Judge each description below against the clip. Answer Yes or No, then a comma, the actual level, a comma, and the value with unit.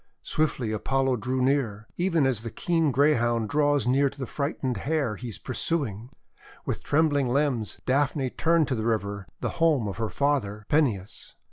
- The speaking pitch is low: Yes, low, 130 Hz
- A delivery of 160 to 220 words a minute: Yes, average, 165 wpm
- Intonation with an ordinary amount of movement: Yes, average, 4.3 semitones